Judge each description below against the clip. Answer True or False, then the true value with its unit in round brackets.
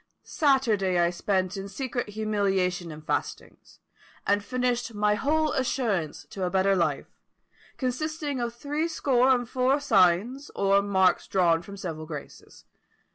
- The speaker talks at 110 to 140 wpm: True (135 wpm)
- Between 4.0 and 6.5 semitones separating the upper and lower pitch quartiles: True (5.6 semitones)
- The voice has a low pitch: False (205 Hz)